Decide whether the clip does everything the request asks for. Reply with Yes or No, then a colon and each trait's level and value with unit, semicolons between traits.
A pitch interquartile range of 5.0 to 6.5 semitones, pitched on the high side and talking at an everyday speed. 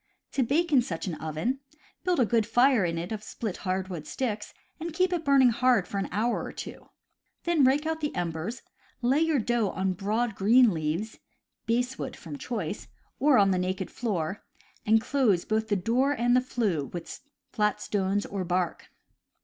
Yes: wide, 5.4 semitones; high, 220 Hz; average, 180 wpm